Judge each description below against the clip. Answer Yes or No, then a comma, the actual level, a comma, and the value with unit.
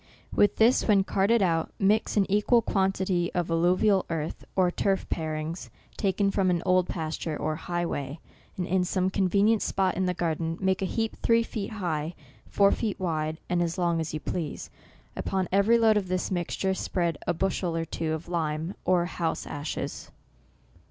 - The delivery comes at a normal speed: Yes, average, 180 wpm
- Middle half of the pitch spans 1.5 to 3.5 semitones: Yes, average, 3.0 semitones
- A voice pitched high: No, medium, 180 Hz